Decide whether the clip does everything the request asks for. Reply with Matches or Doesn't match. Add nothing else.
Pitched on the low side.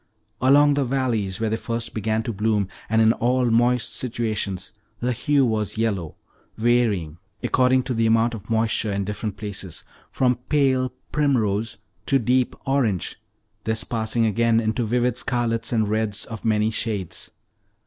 Matches